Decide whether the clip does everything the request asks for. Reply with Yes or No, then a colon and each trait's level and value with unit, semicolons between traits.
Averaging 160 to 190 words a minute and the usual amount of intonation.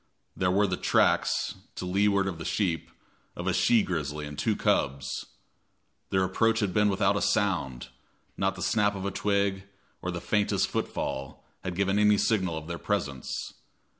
Yes: average, 170 wpm; average, 3.4 semitones